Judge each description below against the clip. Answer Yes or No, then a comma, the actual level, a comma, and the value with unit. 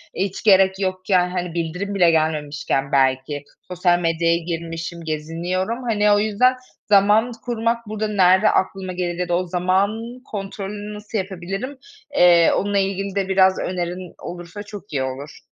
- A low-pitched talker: No, medium, 185 Hz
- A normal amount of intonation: Yes, average, 3.3 semitones